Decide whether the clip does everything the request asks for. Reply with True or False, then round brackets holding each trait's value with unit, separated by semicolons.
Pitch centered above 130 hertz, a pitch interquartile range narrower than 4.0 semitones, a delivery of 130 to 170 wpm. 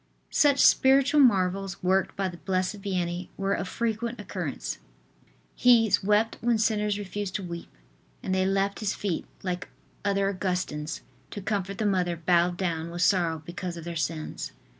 True (190 Hz; 2.8 semitones; 160 wpm)